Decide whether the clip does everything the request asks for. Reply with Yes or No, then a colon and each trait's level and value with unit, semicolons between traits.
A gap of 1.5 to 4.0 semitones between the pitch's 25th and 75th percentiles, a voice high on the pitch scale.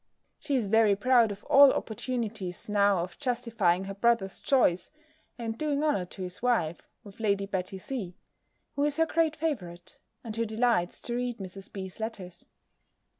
No: average, 4.6 semitones; high, 220 Hz